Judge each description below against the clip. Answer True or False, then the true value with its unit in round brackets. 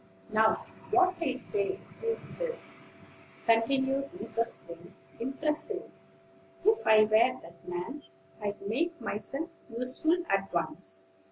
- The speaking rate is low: True (110 wpm)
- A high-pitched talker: True (255 Hz)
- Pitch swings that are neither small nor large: False (7.8 semitones)